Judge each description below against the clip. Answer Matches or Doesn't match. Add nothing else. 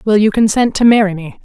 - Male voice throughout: Doesn't match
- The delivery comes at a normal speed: Doesn't match